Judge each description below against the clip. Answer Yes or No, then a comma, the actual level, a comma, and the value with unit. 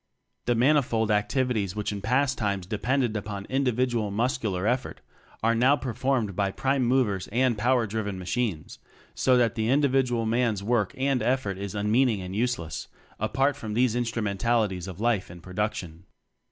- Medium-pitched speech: No, low, 115 Hz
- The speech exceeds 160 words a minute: No, average, 155 wpm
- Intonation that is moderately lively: Yes, average, 3.7 semitones